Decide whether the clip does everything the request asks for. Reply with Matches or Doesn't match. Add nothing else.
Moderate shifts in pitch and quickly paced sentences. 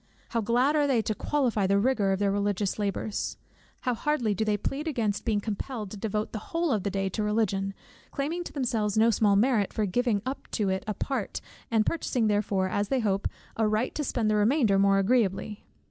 Matches